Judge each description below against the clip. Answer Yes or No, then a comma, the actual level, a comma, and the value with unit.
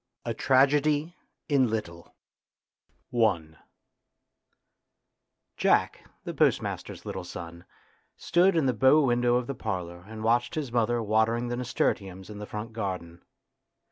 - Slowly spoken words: Yes, slow, 120 wpm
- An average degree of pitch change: Yes, average, 5.0 semitones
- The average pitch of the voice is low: Yes, low, 115 Hz